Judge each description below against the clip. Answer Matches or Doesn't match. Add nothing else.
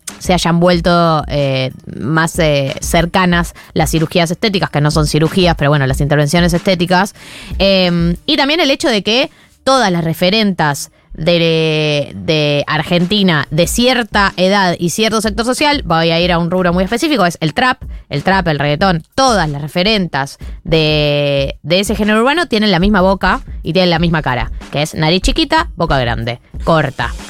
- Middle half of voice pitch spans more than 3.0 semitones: Matches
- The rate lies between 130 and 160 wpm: Doesn't match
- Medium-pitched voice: Matches